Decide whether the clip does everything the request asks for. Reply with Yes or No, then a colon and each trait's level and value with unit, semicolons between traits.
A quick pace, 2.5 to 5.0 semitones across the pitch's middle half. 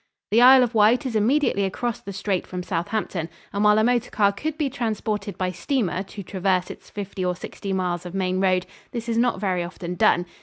Yes: fast, 215 wpm; average, 4.0 semitones